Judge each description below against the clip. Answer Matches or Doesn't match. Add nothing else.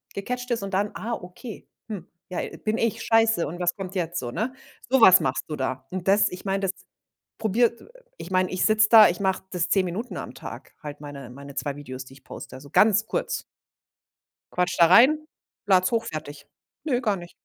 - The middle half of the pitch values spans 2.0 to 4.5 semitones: Doesn't match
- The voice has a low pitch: Doesn't match